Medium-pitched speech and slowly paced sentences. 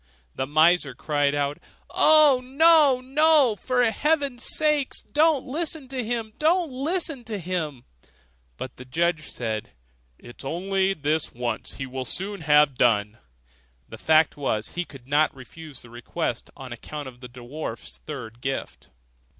No: medium, 160 Hz; average, 150 wpm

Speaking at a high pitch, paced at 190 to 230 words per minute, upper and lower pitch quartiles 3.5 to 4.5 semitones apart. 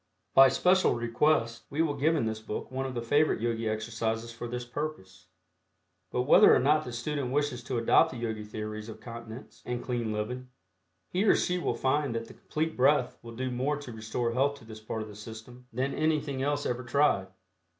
No: low, 120 Hz; fast, 205 wpm; average, 4.0 semitones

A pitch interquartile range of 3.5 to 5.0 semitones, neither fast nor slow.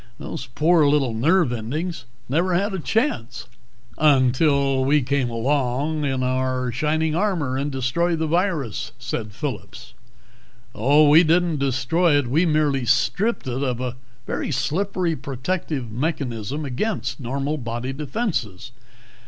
No: average, 4.2 semitones; slow, 130 wpm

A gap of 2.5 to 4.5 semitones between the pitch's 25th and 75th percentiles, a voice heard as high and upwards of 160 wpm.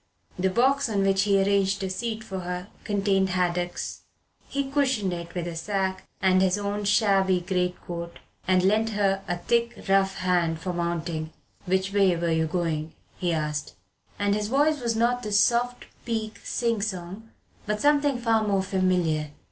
Yes: average, 3.5 semitones; high, 195 Hz; average, 170 wpm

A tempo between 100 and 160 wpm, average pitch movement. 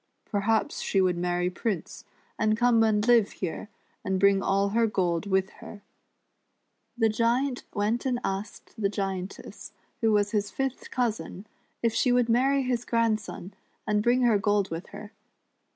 Yes: average, 155 wpm; average, 3.1 semitones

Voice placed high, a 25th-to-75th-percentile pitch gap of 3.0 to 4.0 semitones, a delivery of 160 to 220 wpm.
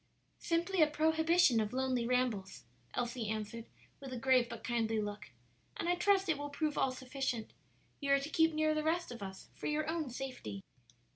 No: very high, 265 Hz; average, 5.1 semitones; average, 190 wpm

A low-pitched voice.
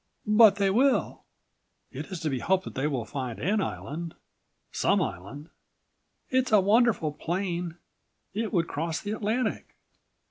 No: medium, 185 Hz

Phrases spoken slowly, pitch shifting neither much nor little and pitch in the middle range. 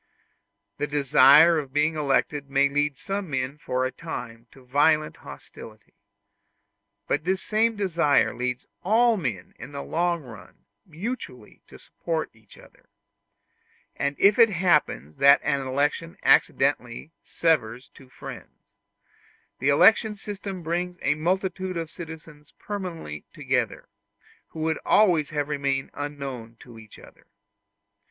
Yes: slow, 130 wpm; average, 4.5 semitones; medium, 150 Hz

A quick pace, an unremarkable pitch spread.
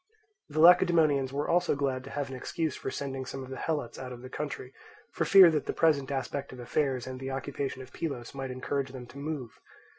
No: fast, 220 wpm; narrow, 2.3 semitones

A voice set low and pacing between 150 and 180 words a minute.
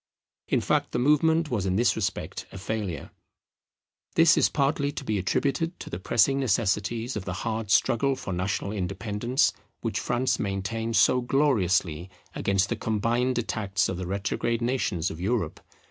Yes: low, 110 Hz; average, 160 wpm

